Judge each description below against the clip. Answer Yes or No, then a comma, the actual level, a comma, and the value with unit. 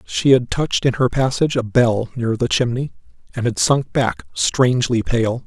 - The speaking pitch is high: No, low, 125 Hz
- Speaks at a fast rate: No, average, 185 wpm